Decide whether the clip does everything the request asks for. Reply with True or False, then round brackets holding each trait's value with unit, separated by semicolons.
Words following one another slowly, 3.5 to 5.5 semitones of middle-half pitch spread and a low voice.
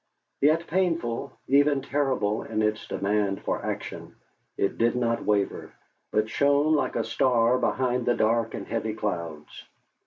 False (145 wpm; 4.8 semitones; 115 Hz)